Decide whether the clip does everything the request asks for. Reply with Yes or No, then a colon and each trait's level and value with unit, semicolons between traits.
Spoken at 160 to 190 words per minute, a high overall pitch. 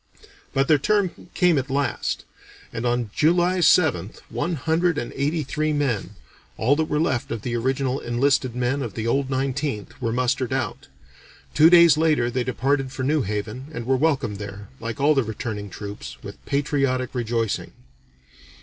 No: average, 170 wpm; low, 130 Hz